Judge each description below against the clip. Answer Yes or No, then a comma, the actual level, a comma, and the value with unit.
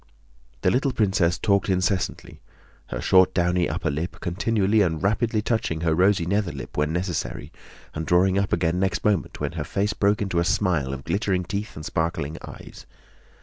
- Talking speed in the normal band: Yes, average, 175 wpm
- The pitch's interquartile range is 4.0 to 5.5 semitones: No, average, 3.3 semitones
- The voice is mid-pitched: No, very low, 95 Hz